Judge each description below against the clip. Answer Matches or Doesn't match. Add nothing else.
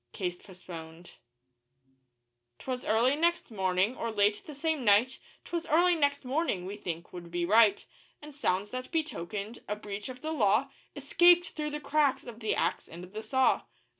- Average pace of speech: Matches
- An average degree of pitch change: Doesn't match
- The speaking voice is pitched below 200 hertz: Doesn't match